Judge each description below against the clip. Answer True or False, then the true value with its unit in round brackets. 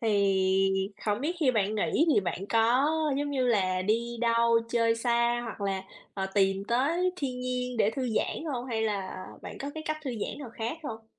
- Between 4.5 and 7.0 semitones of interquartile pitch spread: False (4.0 semitones)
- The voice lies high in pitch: True (230 Hz)